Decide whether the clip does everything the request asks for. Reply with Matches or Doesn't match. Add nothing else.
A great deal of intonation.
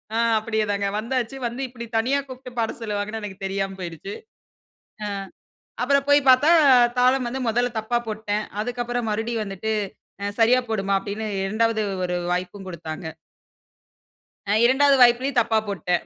Doesn't match